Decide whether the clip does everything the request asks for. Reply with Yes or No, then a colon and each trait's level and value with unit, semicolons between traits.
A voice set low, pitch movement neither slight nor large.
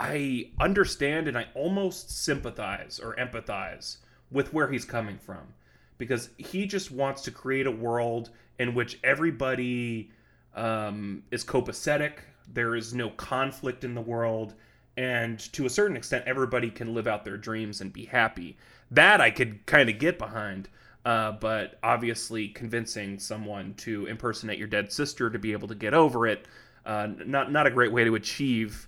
Yes: low, 115 Hz; average, 3.2 semitones